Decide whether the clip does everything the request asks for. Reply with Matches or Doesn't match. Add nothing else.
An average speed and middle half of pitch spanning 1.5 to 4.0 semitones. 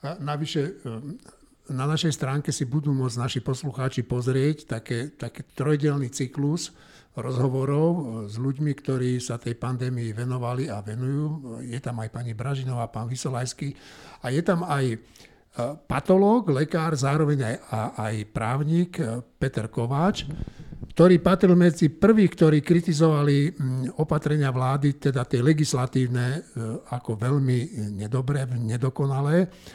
Matches